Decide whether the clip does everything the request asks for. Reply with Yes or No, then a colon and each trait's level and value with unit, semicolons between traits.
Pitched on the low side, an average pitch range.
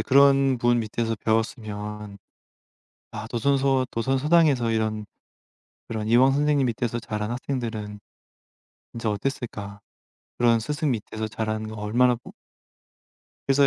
Yes: low, 115 Hz; average, 3.7 semitones